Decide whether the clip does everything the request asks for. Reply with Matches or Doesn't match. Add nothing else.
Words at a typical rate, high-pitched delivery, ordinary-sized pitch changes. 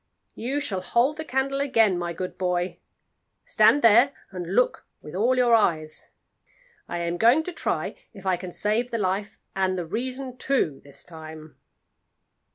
Doesn't match